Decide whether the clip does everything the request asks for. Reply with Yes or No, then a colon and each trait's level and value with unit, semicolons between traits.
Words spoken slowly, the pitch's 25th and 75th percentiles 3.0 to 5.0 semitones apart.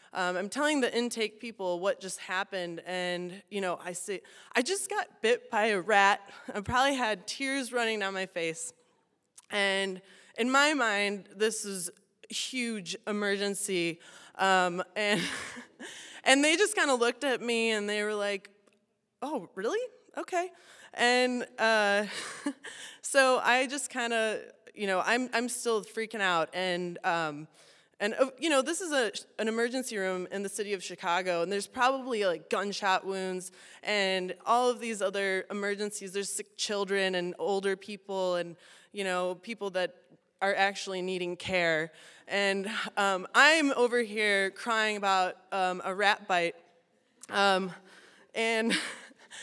No: average, 150 wpm; average, 3.9 semitones